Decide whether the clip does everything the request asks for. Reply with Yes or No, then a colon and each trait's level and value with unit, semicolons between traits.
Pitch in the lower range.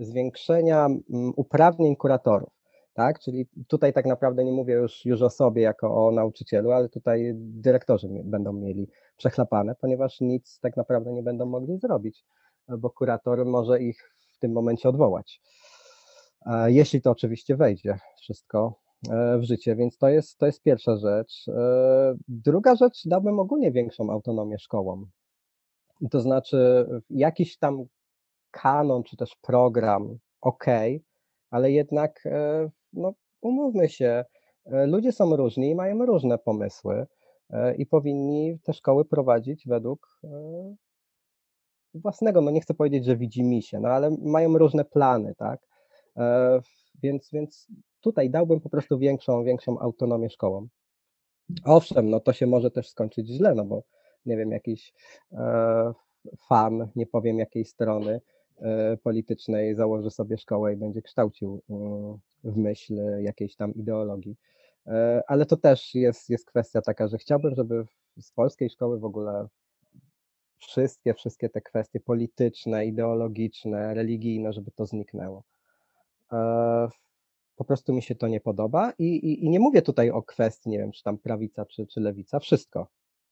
Yes: low, 120 Hz